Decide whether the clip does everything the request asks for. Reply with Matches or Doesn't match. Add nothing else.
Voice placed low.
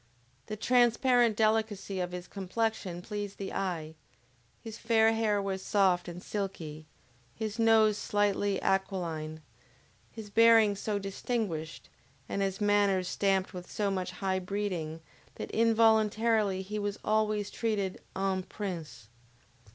Doesn't match